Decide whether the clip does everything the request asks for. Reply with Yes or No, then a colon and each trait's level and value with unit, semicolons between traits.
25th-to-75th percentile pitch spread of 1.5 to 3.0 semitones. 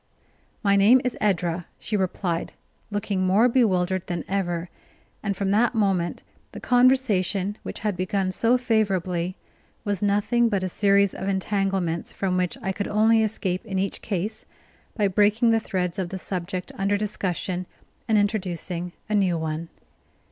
Yes: narrow, 2.6 semitones